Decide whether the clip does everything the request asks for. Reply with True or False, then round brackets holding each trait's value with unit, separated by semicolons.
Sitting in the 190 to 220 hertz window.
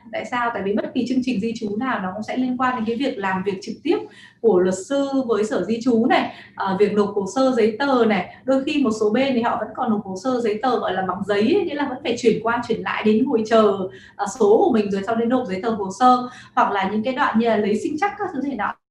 False (230 Hz)